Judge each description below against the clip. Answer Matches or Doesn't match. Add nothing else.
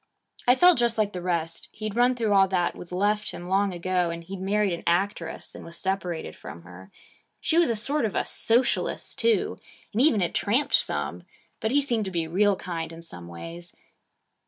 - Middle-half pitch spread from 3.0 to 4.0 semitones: Doesn't match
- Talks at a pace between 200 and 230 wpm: Matches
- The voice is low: Doesn't match